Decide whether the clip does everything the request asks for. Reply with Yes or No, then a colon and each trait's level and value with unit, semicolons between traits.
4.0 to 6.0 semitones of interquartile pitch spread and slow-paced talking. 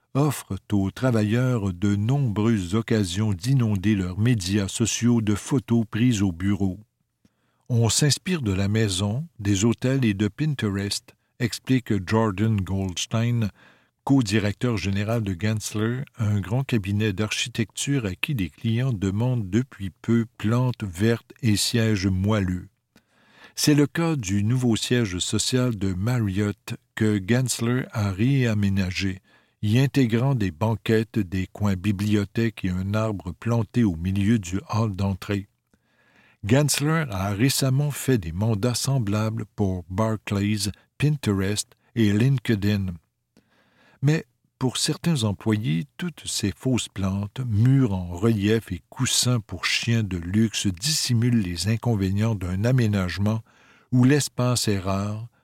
No: average, 3.5 semitones; slow, 125 wpm